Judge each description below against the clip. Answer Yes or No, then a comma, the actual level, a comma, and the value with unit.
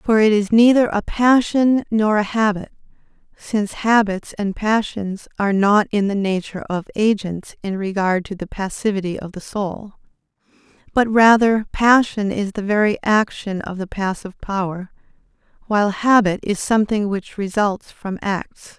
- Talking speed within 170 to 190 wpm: No, average, 150 wpm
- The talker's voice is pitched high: Yes, high, 205 Hz